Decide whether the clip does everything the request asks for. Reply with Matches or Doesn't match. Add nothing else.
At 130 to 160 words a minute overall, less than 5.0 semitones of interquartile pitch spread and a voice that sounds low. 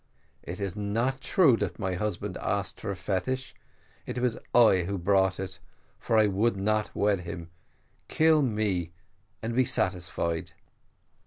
Matches